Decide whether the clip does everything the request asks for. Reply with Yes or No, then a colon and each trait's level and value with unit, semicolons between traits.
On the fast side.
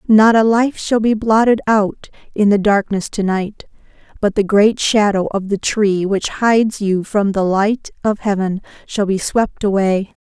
No: average, 175 wpm